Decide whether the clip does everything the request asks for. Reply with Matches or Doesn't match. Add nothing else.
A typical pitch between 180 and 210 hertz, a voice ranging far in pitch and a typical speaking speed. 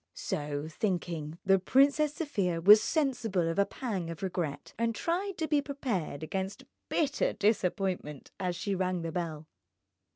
Matches